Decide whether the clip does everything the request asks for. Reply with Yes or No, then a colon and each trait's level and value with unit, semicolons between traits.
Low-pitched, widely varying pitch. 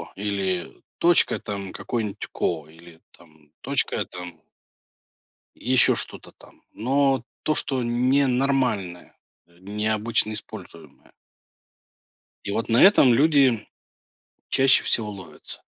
Yes: low, 110 Hz; wide, 5.9 semitones